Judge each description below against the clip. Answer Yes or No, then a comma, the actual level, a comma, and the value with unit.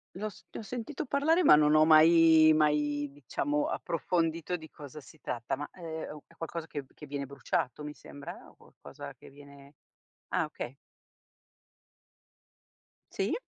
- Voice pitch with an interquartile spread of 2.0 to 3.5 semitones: Yes, narrow, 2.5 semitones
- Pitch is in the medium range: Yes, medium, 155 Hz